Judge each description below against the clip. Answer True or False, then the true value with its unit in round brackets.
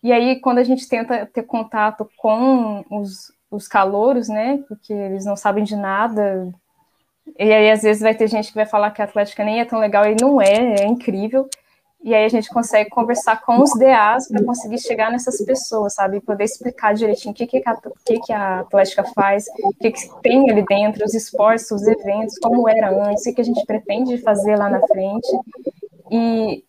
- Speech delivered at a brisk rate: True (210 wpm)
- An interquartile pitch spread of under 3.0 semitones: True (2.4 semitones)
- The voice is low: False (215 Hz)